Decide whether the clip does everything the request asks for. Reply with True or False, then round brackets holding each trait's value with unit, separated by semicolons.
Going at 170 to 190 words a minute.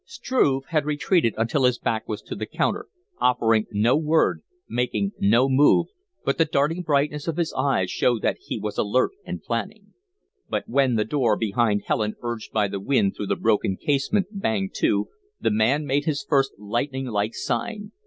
True (180 wpm)